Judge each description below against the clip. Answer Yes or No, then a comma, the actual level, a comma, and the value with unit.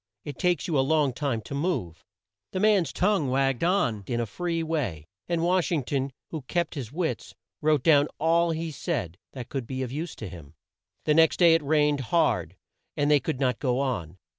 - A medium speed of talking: No, fast, 210 wpm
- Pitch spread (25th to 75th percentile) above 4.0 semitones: Yes, average, 4.7 semitones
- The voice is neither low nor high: Yes, medium, 145 Hz